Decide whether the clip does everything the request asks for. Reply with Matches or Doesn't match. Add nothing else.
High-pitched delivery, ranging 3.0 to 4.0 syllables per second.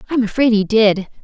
Doesn't match